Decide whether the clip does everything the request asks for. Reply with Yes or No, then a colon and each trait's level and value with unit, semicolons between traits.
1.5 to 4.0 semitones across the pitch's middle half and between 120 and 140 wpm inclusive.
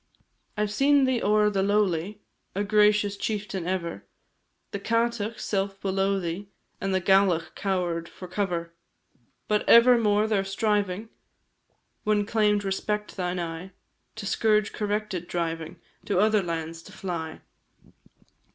Yes: average, 2.8 semitones; slow, 135 wpm